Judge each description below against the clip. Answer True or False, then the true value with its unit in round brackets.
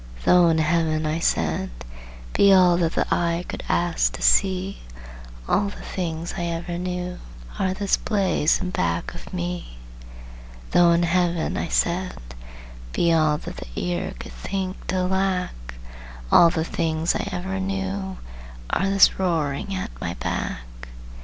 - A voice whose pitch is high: False (175 Hz)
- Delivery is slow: False (150 wpm)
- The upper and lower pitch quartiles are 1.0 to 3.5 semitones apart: True (2.9 semitones)